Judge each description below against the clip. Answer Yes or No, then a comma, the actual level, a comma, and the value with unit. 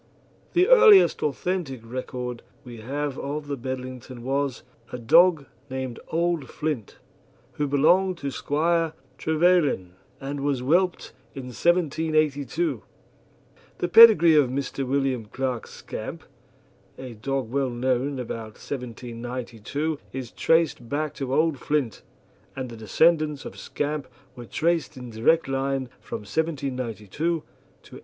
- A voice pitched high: No, medium, 140 Hz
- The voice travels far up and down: No, average, 4.0 semitones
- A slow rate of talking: Yes, slow, 125 wpm